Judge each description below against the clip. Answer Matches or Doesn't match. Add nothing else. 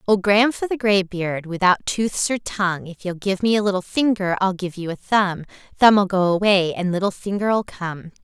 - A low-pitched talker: Doesn't match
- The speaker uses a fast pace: Doesn't match